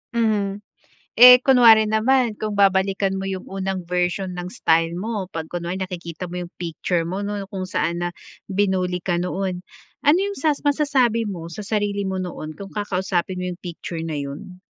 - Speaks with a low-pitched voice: No, high, 190 Hz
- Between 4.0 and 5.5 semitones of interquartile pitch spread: No, average, 3.1 semitones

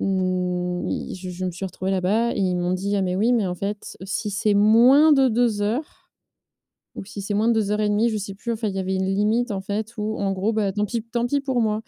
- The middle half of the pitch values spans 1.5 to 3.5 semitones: Yes, average, 3.0 semitones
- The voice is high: Yes, high, 205 Hz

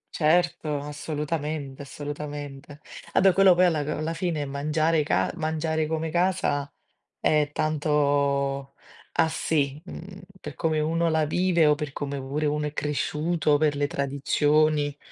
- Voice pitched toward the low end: No, medium, 150 Hz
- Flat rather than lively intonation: Yes, narrow, 1.8 semitones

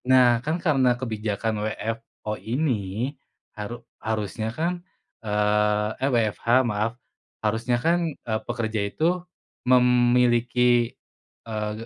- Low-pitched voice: Yes, low, 115 Hz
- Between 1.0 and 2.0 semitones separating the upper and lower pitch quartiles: No, narrow, 2.5 semitones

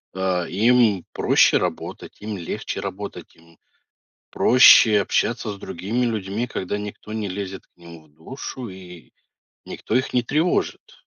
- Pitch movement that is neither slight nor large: Yes, average, 4.1 semitones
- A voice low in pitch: Yes, low, 100 Hz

